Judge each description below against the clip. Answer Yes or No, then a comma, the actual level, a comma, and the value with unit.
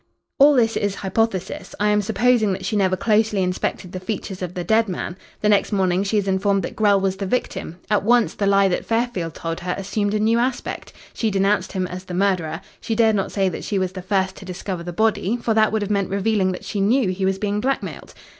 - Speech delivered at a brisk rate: Yes, fast, 240 wpm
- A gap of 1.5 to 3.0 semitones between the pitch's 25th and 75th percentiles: Yes, narrow, 2.6 semitones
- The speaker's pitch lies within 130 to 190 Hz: No, high, 200 Hz